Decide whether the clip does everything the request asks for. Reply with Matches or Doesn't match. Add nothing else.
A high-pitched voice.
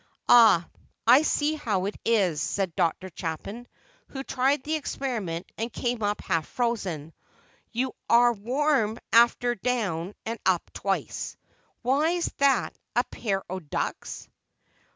Matches